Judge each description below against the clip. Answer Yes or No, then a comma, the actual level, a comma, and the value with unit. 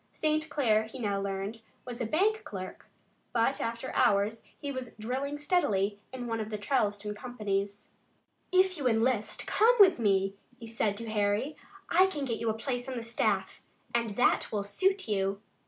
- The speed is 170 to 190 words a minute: Yes, average, 180 wpm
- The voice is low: No, high, 230 Hz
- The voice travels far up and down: No, average, 4.8 semitones